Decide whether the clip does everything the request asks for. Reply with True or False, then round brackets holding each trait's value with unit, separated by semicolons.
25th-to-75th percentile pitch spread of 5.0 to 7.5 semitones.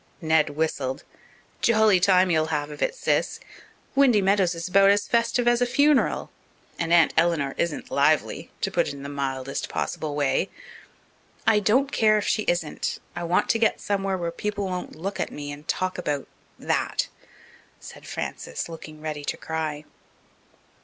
True (5.3 semitones)